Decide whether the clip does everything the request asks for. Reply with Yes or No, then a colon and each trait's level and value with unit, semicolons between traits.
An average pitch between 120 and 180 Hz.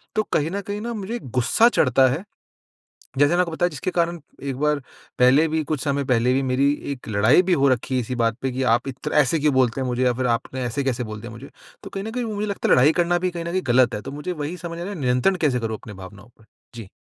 Yes: low, 135 Hz